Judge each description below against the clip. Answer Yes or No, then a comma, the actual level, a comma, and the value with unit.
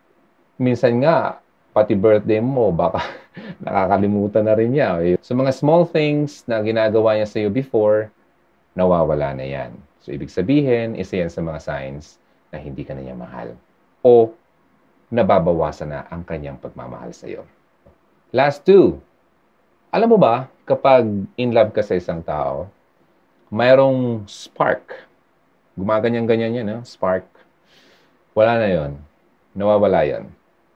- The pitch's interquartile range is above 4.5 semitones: No, average, 4.1 semitones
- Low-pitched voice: Yes, low, 110 Hz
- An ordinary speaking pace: Yes, average, 130 wpm